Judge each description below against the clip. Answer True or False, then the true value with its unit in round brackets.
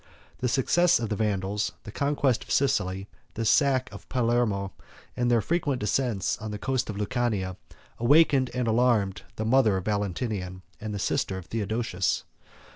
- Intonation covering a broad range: False (4.1 semitones)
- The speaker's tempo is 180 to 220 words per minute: False (160 wpm)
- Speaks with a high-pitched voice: False (110 Hz)